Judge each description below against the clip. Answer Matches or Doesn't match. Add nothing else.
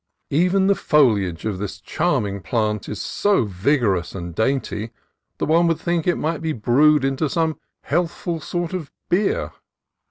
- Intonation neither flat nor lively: Doesn't match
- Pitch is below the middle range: Doesn't match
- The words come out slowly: Doesn't match